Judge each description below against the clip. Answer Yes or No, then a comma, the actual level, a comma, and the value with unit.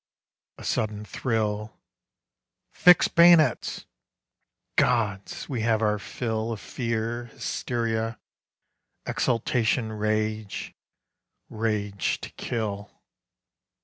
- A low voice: Yes, low, 110 Hz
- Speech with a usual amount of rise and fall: No, narrow, 1.7 semitones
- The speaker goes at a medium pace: No, slow, 80 wpm